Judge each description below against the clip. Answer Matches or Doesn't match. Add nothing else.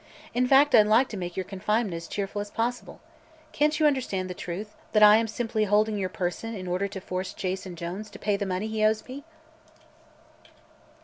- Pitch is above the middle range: Matches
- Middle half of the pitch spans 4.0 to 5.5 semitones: Doesn't match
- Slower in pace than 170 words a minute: Doesn't match